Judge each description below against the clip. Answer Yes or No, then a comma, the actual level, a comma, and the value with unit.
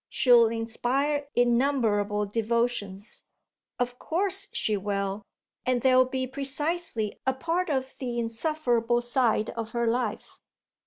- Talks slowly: Yes, slow, 115 wpm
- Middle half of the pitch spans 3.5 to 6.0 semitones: No, average, 2.9 semitones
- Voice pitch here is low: No, high, 240 Hz